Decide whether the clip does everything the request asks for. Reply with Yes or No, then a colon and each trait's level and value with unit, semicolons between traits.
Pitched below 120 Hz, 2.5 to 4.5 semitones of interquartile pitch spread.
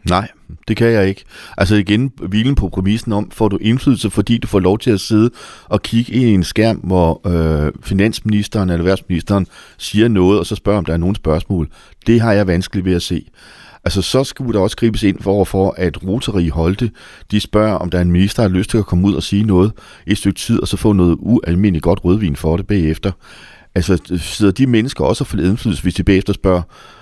Yes: low, 100 Hz; average, 3.1 semitones